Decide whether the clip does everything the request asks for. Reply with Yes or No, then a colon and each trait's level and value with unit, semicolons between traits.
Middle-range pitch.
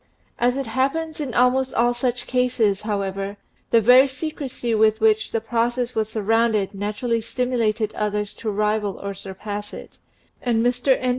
No: high, 230 Hz